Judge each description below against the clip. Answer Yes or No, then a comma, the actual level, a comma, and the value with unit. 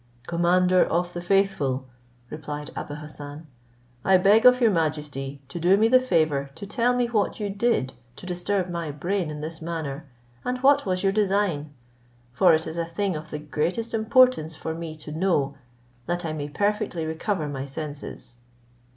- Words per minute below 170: No, average, 175 wpm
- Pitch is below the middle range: No, medium, 170 Hz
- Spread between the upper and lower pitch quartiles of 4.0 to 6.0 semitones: Yes, average, 4.9 semitones